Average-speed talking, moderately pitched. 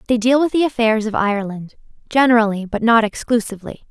No: average, 155 wpm; high, 225 Hz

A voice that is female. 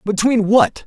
No: male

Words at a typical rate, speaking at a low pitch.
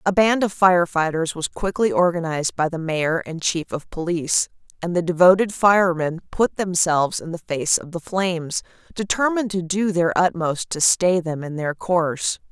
No: average, 180 wpm; medium, 175 Hz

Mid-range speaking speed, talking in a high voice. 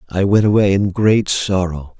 No: average, 180 wpm; very low, 95 Hz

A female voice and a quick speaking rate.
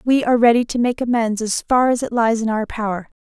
Yes: female; fast, 260 wpm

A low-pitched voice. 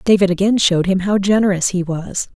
No: high, 190 Hz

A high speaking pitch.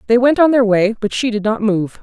Yes: high, 225 Hz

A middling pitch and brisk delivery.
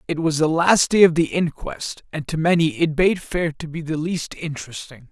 Yes: medium, 160 Hz; fast, 225 wpm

